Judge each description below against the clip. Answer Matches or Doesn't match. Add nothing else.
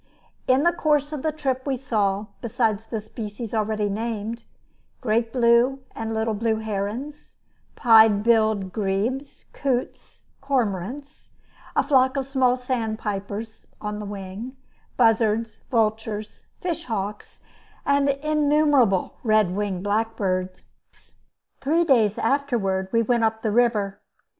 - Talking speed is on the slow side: Matches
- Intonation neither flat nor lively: Matches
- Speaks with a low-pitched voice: Doesn't match